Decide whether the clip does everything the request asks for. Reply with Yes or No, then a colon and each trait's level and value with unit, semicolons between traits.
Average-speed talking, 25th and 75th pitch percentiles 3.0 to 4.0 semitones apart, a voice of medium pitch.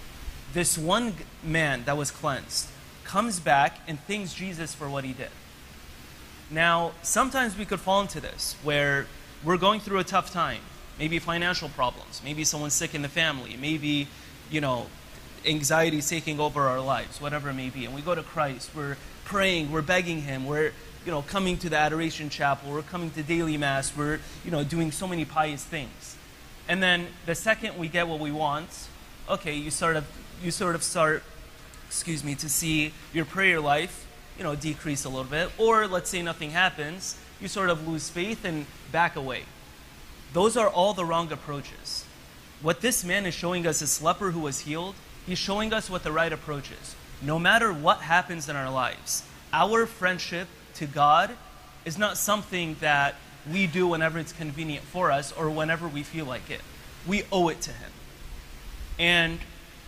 Yes: average, 185 wpm; average, 3.6 semitones; medium, 155 Hz